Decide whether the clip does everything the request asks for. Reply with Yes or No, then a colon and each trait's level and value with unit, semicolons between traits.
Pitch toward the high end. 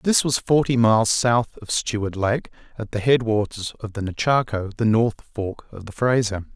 No: low, 115 Hz